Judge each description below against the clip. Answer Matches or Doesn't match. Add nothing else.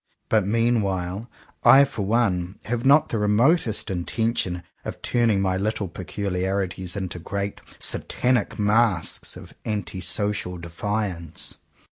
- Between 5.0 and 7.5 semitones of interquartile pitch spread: Doesn't match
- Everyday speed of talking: Doesn't match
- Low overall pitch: Matches